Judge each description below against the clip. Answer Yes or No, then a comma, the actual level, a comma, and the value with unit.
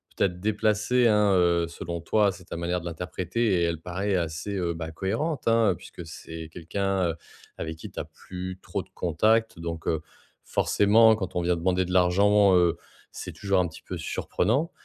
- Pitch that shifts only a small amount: No, average, 3.3 semitones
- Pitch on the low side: Yes, very low, 90 Hz